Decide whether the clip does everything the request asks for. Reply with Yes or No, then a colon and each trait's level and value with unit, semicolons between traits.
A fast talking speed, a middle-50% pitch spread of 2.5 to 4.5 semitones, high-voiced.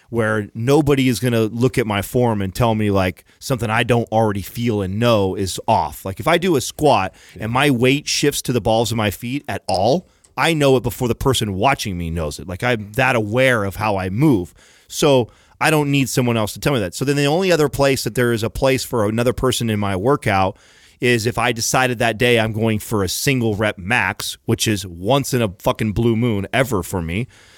No: fast, 235 wpm; average, 3.6 semitones; low, 115 Hz